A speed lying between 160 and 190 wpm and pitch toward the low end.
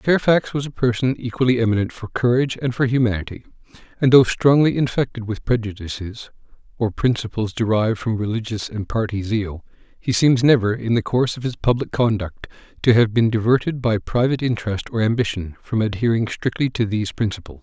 Yes: average, 170 wpm; low, 115 Hz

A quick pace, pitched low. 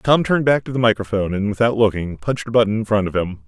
Yes: fast, 275 wpm; low, 110 Hz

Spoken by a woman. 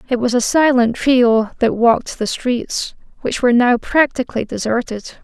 Yes: female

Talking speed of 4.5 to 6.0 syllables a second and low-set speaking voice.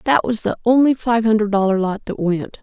No: 5.5 syllables/s; high, 220 Hz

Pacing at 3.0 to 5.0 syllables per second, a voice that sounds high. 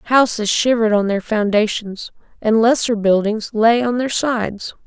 Yes: 4.5 syllables/s; high, 220 Hz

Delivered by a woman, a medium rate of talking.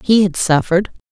Yes: female; average, 160 wpm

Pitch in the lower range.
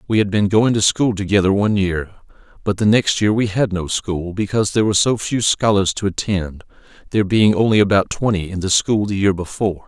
Yes: low, 100 Hz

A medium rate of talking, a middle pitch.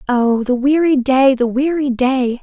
No: average, 175 wpm; very high, 260 Hz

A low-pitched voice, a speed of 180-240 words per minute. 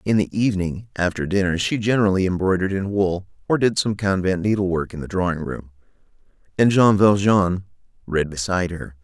No: very low, 95 Hz; average, 165 wpm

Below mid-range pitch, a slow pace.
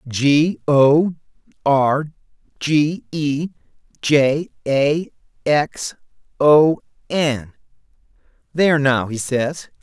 No: medium, 145 Hz; slow, 90 wpm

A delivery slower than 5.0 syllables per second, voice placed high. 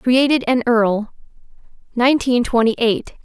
Yes: 4.6 syllables/s; high, 240 Hz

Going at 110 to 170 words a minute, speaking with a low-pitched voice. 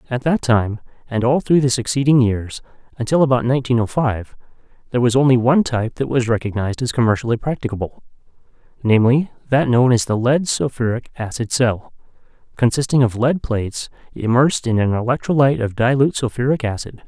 Yes: average, 160 wpm; low, 120 Hz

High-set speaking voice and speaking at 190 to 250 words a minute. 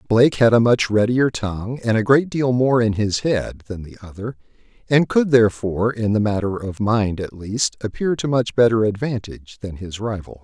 No: low, 115 Hz; average, 200 wpm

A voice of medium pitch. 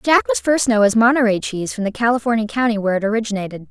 No: high, 225 Hz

